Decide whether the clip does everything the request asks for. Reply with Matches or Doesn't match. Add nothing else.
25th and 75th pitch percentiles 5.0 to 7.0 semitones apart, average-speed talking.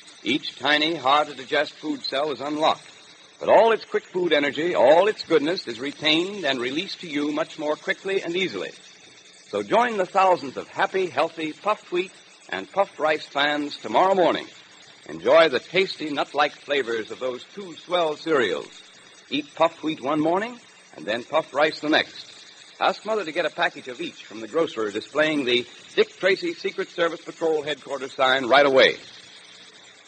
Matches